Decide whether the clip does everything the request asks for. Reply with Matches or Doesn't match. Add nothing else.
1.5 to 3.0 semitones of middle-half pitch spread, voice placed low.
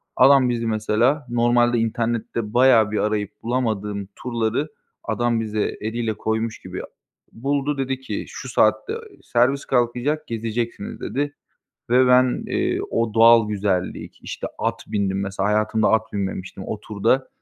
Matches